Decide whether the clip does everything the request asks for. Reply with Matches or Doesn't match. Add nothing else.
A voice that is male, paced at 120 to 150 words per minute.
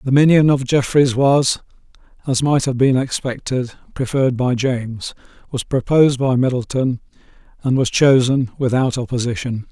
Matches